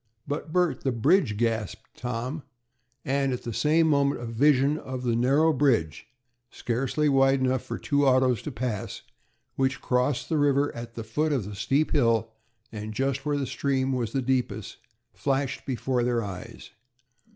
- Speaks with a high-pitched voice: No, low, 130 Hz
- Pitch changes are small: No, average, 3.3 semitones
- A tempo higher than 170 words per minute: No, average, 165 wpm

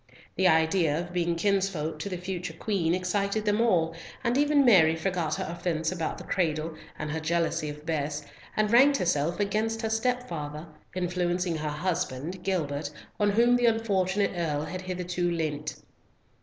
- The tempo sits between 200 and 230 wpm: No, average, 160 wpm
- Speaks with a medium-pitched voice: Yes, medium, 175 Hz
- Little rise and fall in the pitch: No, average, 4.0 semitones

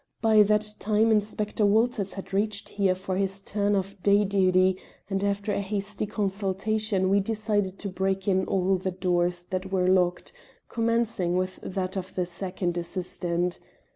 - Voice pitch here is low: No, high, 195 Hz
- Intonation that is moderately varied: No, narrow, 2.0 semitones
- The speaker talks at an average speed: Yes, average, 160 wpm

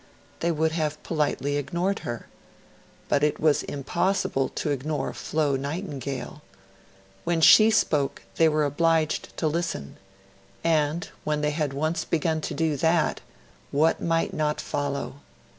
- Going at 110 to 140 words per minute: Yes, slow, 135 wpm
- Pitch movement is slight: Yes, narrow, 2.3 semitones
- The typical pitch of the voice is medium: Yes, medium, 155 Hz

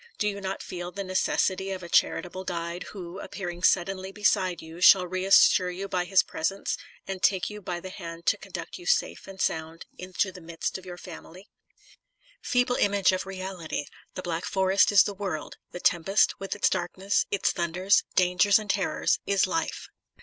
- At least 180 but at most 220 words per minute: Yes, average, 185 wpm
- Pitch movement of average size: No, narrow, 1.9 semitones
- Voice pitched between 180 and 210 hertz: Yes, medium, 185 Hz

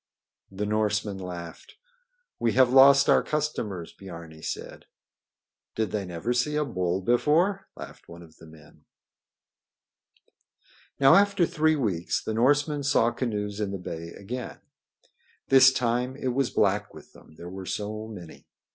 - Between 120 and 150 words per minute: Yes, average, 145 wpm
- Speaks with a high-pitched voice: No, low, 110 Hz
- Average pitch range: No, wide, 6.4 semitones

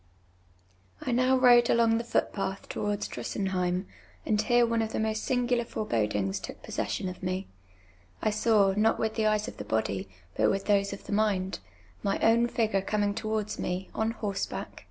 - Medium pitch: No, high, 210 Hz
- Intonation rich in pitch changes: No, average, 2.8 semitones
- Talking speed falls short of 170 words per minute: No, average, 185 wpm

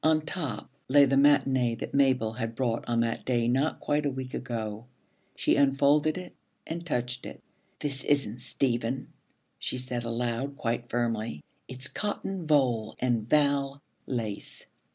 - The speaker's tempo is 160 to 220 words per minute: No, average, 150 wpm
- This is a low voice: Yes, low, 130 Hz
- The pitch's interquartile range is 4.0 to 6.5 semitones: No, average, 3.3 semitones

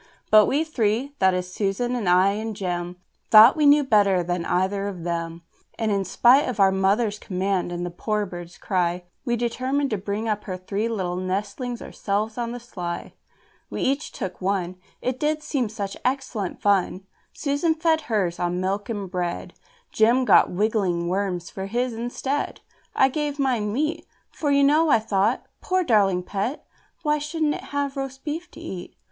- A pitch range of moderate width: No, wide, 6.0 semitones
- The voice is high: Yes, high, 210 Hz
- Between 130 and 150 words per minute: No, average, 180 wpm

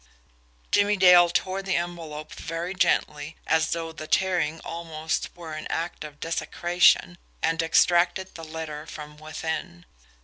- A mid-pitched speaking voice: Yes, medium, 165 Hz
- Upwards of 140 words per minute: No, slow, 135 wpm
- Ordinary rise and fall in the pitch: No, narrow, 2.1 semitones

